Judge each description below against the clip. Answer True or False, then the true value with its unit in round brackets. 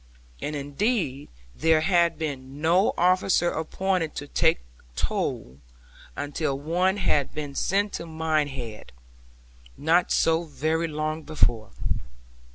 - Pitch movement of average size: True (3.1 semitones)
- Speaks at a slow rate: True (110 wpm)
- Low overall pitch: False (155 Hz)